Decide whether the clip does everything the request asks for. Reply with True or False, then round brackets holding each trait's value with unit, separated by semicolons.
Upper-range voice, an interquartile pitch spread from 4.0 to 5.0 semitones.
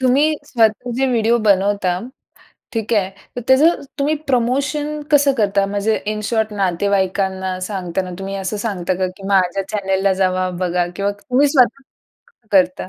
True (205 Hz; 4.6 semitones)